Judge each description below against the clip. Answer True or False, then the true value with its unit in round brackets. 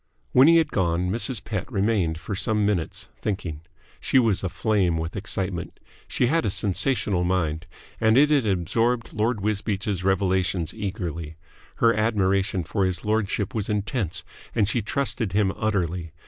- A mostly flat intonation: False (3.4 semitones)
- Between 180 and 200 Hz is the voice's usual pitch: False (100 Hz)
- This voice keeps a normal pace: True (150 wpm)